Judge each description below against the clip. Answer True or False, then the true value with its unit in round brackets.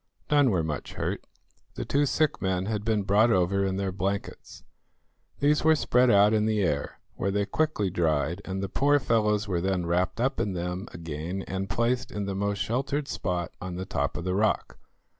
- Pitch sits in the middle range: False (100 Hz)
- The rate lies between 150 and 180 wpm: False (195 wpm)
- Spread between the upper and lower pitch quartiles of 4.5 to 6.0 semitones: False (3.9 semitones)